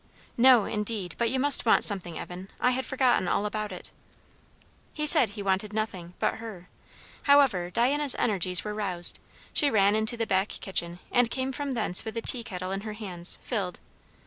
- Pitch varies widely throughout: No, average, 4.6 semitones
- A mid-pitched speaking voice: No, high, 215 Hz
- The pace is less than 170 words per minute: No, average, 185 wpm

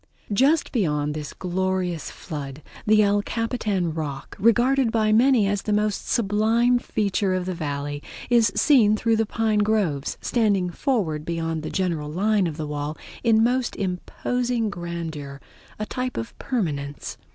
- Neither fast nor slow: Yes, average, 150 wpm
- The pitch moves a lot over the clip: Yes, wide, 5.9 semitones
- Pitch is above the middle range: Yes, high, 200 Hz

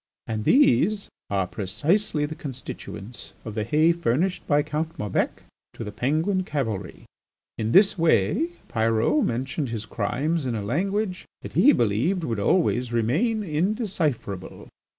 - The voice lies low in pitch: No, medium, 145 Hz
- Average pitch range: No, wide, 8.3 semitones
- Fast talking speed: No, slow, 135 wpm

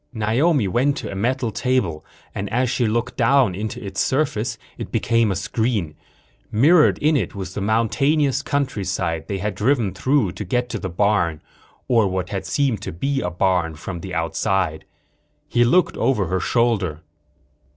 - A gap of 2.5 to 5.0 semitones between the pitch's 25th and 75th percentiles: No, wide, 5.4 semitones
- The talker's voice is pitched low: Yes, low, 110 Hz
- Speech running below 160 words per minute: No, average, 170 wpm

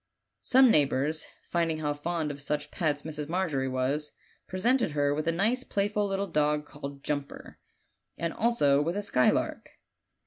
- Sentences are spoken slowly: No, average, 150 wpm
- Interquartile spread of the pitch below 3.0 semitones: No, average, 4.6 semitones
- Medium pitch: Yes, medium, 155 Hz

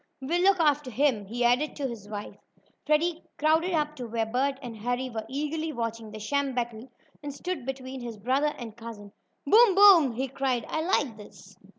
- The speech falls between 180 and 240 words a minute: Yes, average, 190 wpm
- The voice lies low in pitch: No, very high, 260 Hz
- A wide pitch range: No, average, 4.7 semitones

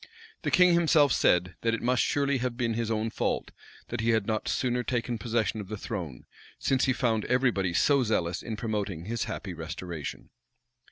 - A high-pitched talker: No, low, 115 Hz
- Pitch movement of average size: Yes, average, 4.1 semitones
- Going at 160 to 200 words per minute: Yes, average, 190 wpm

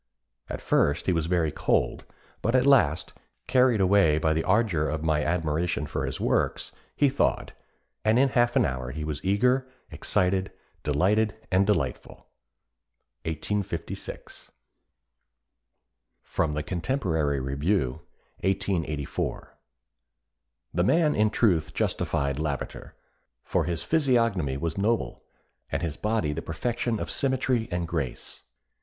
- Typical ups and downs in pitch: No, wide, 6.5 semitones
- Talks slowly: Yes, slow, 125 wpm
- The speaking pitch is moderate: No, very low, 90 Hz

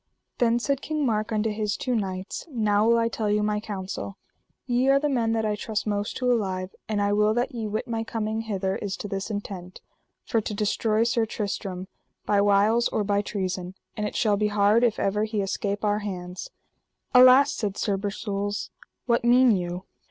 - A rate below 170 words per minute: No, average, 195 wpm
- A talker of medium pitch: No, high, 210 Hz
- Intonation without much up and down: Yes, narrow, 2.3 semitones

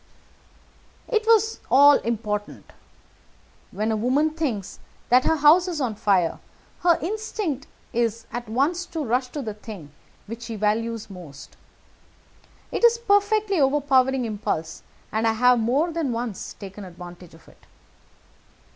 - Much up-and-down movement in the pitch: Yes, wide, 6.8 semitones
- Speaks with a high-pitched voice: Yes, high, 245 Hz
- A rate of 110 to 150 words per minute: Yes, average, 140 wpm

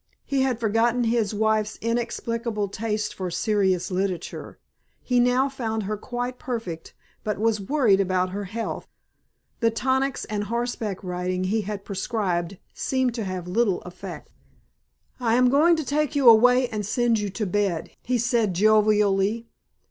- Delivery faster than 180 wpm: No, average, 150 wpm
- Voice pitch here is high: Yes, high, 220 Hz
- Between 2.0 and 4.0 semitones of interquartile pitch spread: Yes, average, 3.5 semitones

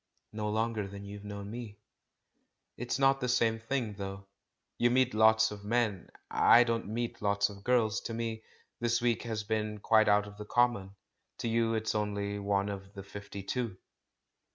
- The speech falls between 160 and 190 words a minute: Yes, average, 175 wpm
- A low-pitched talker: Yes, low, 110 Hz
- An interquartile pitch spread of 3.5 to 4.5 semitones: No, narrow, 2.4 semitones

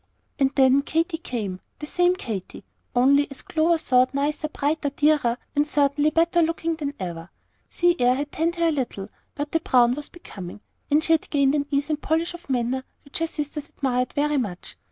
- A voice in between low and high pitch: No, very high, 290 Hz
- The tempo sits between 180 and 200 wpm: Yes, average, 195 wpm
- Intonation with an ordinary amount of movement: Yes, average, 3.7 semitones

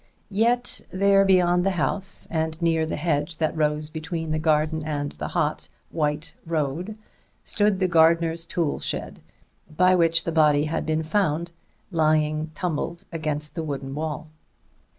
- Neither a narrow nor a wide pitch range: No, narrow, 2.2 semitones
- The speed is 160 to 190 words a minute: No, average, 150 wpm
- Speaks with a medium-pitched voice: Yes, medium, 160 Hz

